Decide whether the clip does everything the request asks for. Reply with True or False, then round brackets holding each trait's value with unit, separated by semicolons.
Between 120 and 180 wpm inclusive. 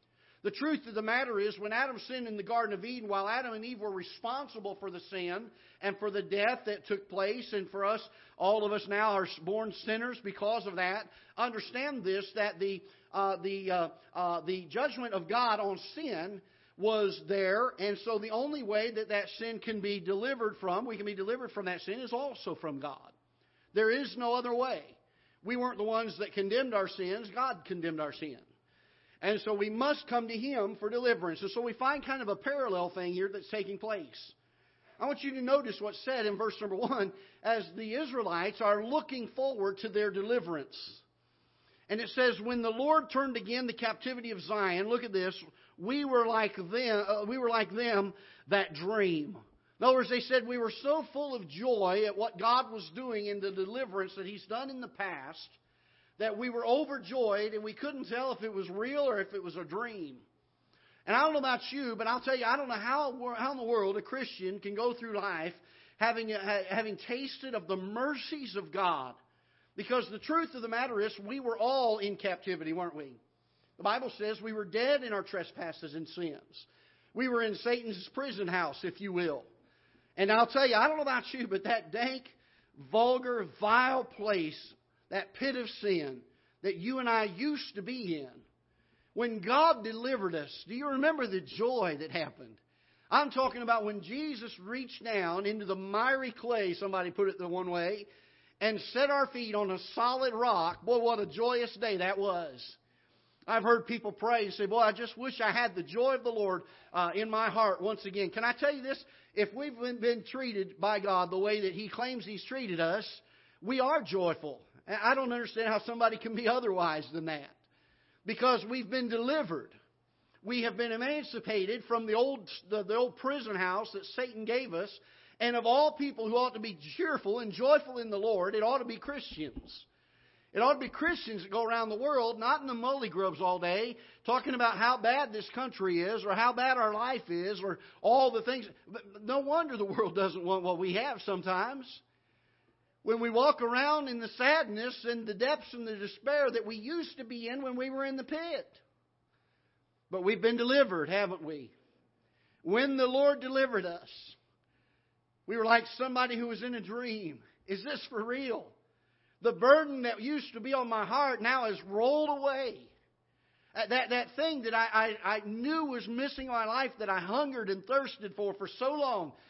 False (200 wpm)